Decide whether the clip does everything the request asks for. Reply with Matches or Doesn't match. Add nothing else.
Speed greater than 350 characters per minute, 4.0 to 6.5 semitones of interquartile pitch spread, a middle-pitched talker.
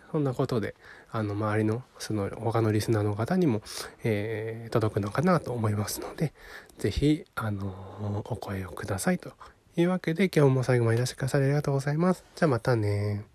Doesn't match